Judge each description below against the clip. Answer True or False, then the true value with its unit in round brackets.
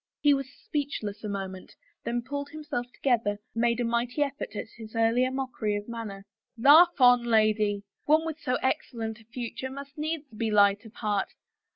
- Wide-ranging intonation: False (4.4 semitones)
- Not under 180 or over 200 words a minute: True (185 wpm)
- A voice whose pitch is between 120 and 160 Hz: False (235 Hz)